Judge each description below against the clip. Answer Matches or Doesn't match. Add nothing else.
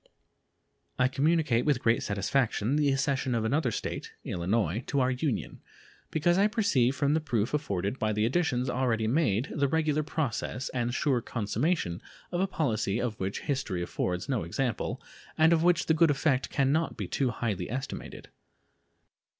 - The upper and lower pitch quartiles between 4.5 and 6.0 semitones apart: Matches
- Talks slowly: Doesn't match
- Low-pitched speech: Matches